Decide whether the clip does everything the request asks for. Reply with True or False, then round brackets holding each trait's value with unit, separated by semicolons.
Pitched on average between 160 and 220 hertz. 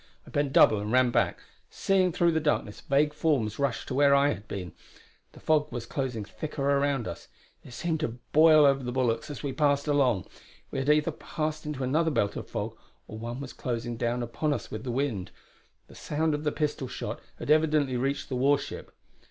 False (140 Hz)